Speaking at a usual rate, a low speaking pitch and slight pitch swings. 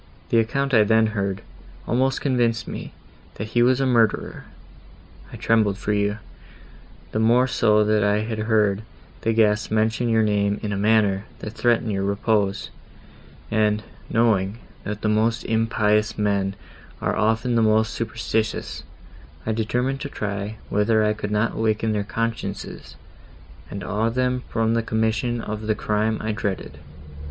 Yes: average, 150 wpm; low, 110 Hz; narrow, 1.5 semitones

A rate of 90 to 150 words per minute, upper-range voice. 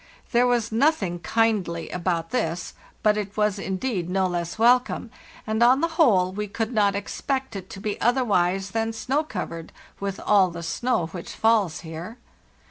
No: average, 165 wpm; high, 210 Hz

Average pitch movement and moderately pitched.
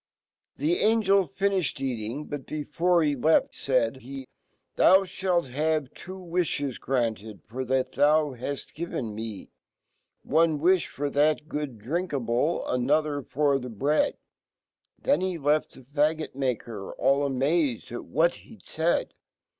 Yes: average, 4.1 semitones; medium, 145 Hz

